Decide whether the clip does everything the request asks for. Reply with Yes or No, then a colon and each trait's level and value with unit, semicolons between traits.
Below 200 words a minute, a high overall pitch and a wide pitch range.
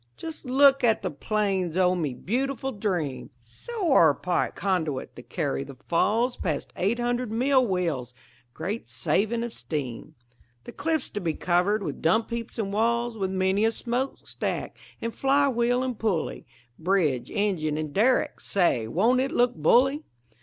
Yes: average, 160 wpm; high, 205 Hz; wide, 6.2 semitones